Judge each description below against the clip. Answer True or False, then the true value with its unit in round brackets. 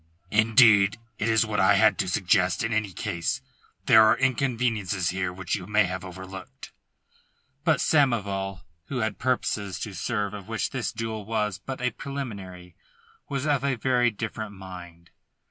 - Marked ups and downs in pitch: False (4.0 semitones)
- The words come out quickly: False (160 wpm)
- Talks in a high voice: False (105 Hz)